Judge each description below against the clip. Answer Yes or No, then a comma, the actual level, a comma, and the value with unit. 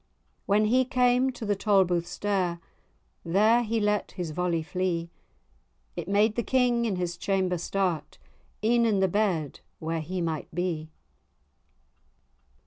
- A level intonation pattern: No, average, 4.0 semitones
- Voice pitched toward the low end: No, high, 190 Hz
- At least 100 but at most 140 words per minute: Yes, slow, 135 wpm